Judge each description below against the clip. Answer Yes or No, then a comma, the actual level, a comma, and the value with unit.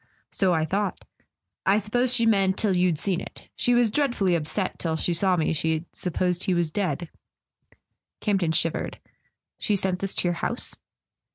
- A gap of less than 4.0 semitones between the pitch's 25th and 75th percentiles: Yes, average, 3.4 semitones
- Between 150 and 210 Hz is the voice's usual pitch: Yes, medium, 185 Hz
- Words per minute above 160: Yes, average, 175 wpm